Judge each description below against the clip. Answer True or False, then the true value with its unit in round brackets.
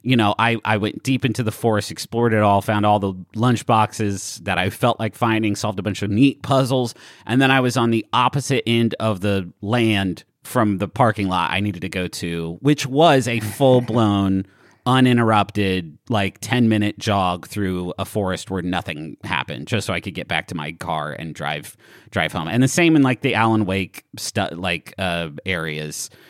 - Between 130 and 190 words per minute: False (205 wpm)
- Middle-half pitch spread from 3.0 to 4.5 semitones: True (4.0 semitones)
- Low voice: True (105 Hz)